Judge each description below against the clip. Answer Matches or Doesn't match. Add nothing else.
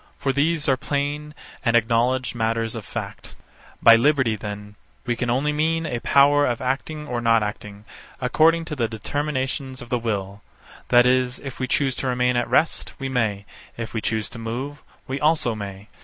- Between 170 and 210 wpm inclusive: Matches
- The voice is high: Doesn't match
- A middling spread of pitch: Matches